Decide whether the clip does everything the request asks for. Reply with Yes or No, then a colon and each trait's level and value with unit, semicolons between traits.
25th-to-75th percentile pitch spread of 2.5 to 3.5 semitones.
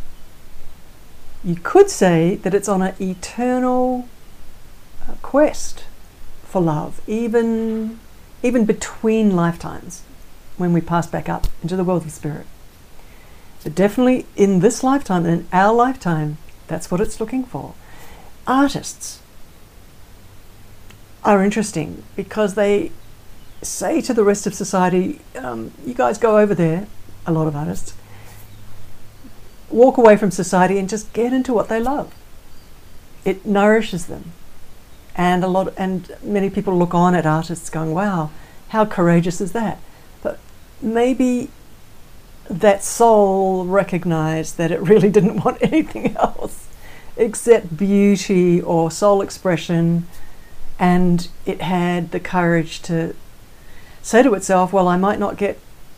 No: average, 4.5 semitones